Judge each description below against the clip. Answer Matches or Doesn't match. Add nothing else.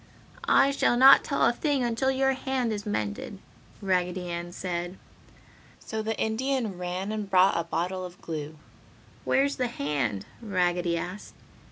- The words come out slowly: Doesn't match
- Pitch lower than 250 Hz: Matches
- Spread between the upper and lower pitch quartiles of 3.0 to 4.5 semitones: Doesn't match